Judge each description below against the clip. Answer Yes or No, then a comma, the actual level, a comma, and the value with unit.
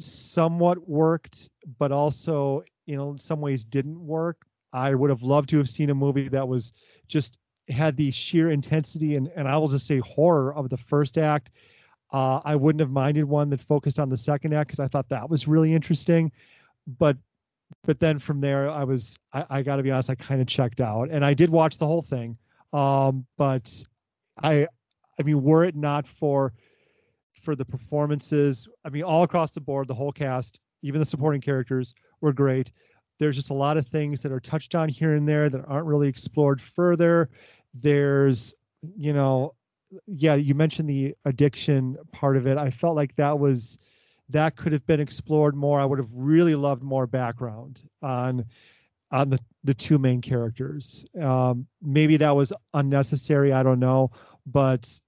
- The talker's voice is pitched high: No, medium, 140 Hz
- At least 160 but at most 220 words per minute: Yes, average, 185 wpm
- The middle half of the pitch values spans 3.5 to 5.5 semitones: No, narrow, 2.5 semitones